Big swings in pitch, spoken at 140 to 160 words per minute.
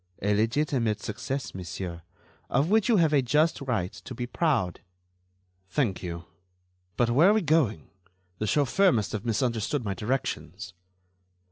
Yes: wide, 6.5 semitones; average, 145 wpm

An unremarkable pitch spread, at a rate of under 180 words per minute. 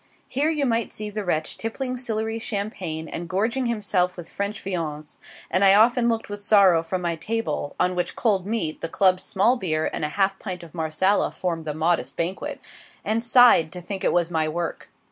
No: average, 4.8 semitones; average, 200 wpm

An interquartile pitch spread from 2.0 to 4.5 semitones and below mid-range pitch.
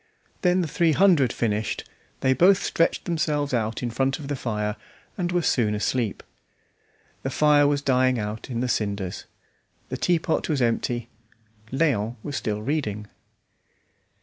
No: wide, 5.5 semitones; low, 130 Hz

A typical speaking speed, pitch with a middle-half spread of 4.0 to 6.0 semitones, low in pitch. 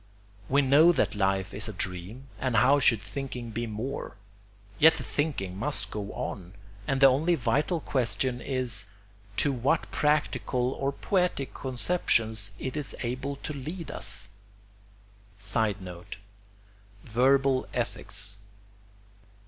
No: slow, 125 wpm; average, 4.8 semitones; low, 130 Hz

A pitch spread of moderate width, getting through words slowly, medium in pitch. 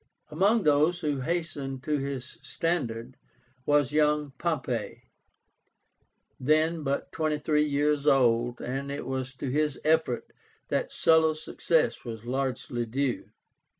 Yes: average, 3.0 semitones; slow, 120 wpm; medium, 145 Hz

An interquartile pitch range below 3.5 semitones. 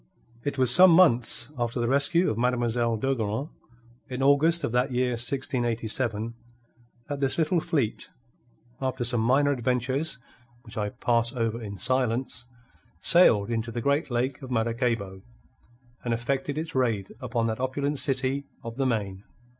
Yes: average, 2.9 semitones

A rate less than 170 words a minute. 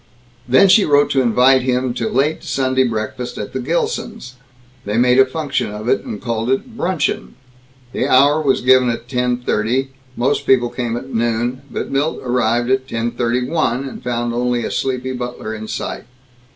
No: average, 180 wpm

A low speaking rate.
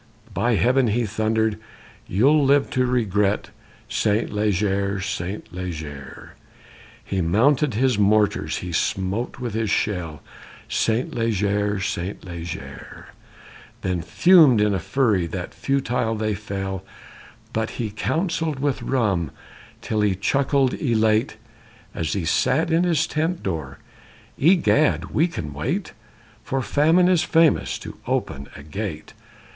Yes: slow, 130 wpm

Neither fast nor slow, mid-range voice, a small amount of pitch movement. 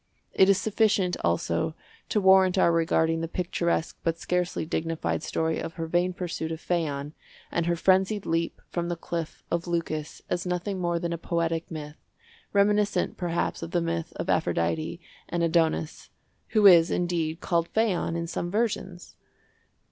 Yes: average, 155 wpm; medium, 170 Hz; narrow, 1.8 semitones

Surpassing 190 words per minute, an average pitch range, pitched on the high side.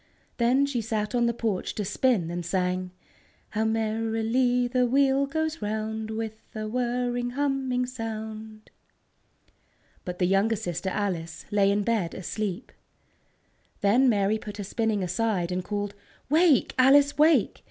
No: average, 140 wpm; average, 3.6 semitones; high, 220 Hz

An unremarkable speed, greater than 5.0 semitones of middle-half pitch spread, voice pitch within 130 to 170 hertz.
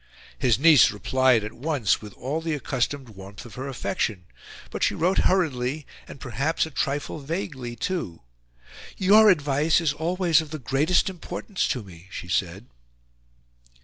Yes: average, 150 wpm; wide, 5.5 semitones; medium, 140 Hz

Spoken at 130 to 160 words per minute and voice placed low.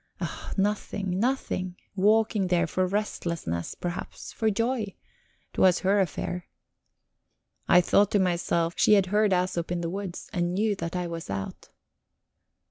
No: average, 140 wpm; medium, 185 Hz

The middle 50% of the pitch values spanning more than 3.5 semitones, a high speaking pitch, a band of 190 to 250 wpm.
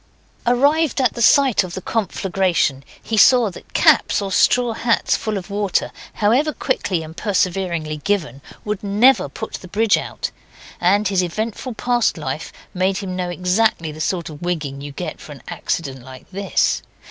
No: average, 4.6 semitones; high, 195 Hz; average, 170 wpm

